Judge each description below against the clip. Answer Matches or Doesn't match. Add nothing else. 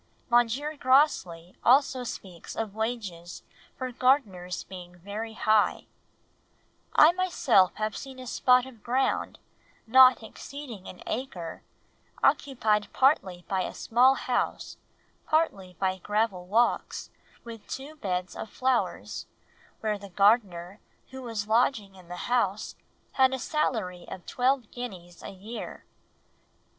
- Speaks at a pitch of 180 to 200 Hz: Doesn't match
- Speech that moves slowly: Matches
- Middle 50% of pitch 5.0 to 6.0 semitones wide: Matches